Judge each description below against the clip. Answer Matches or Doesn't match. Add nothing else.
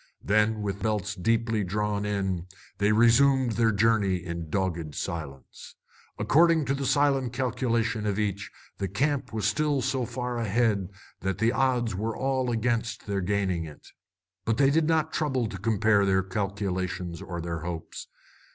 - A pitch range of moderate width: Matches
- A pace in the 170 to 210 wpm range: Doesn't match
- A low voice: Matches